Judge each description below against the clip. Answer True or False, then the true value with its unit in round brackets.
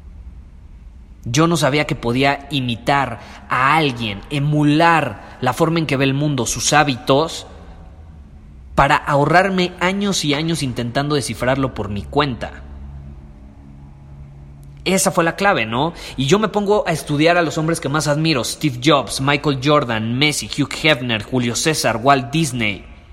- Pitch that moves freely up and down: True (8.7 semitones)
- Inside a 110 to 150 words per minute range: True (145 wpm)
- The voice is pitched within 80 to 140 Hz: True (135 Hz)